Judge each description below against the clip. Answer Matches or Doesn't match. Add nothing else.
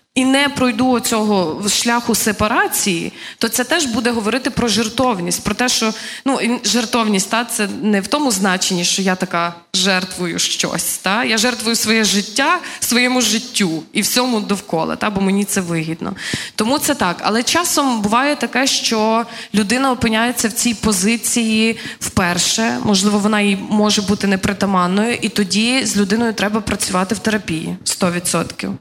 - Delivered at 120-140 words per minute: Doesn't match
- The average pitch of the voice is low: Doesn't match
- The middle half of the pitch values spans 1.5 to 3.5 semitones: Matches